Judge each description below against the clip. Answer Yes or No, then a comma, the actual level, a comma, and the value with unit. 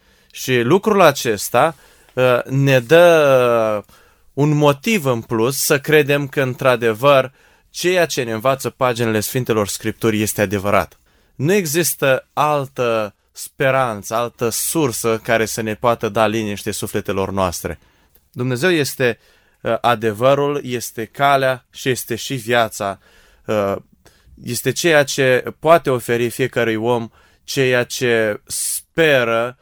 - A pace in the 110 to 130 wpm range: Yes, average, 120 wpm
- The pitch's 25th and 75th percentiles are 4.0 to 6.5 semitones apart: No, average, 3.6 semitones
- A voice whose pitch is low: Yes, low, 125 Hz